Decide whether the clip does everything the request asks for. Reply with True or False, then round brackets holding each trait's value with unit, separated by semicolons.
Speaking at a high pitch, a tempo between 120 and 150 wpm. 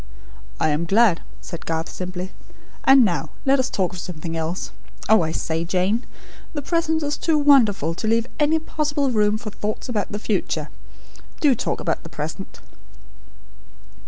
False (215 Hz; 160 wpm)